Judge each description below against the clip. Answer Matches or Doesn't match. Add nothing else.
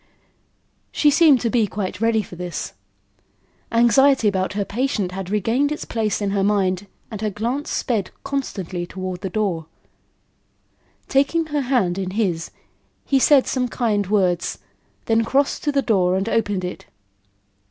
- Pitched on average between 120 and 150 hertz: Doesn't match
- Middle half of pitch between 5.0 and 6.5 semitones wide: Matches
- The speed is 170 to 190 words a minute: Doesn't match